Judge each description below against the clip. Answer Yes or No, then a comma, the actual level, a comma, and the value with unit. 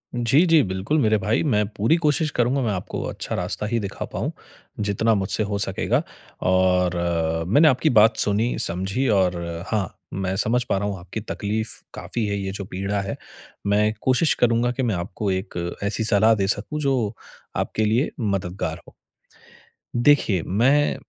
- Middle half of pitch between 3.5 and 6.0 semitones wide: Yes, average, 3.8 semitones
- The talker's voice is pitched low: Yes, low, 105 Hz